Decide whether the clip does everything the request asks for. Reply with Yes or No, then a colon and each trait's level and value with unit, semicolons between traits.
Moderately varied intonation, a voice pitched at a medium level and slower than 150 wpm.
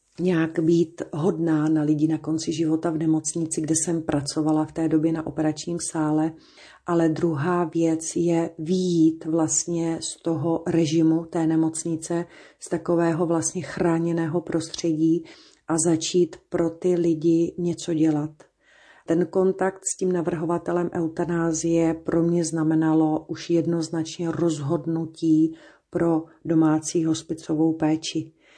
No: narrow, 1.2 semitones; medium, 165 Hz; average, 120 wpm